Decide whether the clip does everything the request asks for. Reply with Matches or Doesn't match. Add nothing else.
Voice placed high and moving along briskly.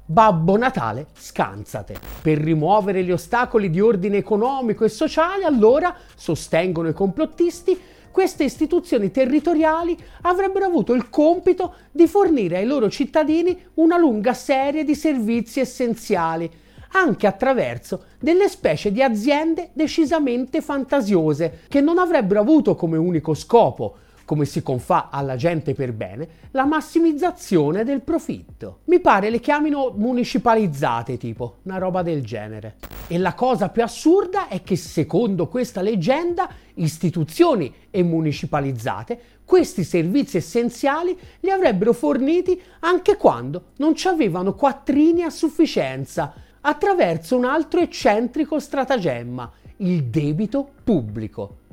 Doesn't match